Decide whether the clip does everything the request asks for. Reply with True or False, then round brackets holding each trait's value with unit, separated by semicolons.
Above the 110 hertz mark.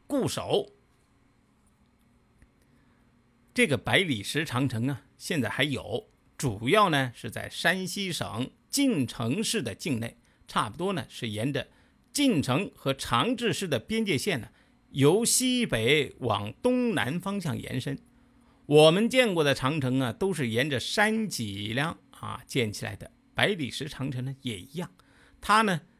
True (140 Hz)